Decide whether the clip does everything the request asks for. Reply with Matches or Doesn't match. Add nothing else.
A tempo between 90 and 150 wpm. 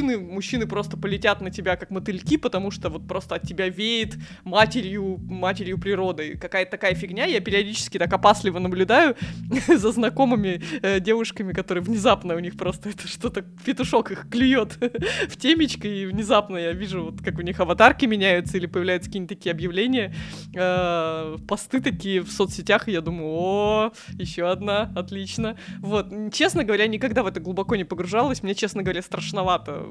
Doesn't match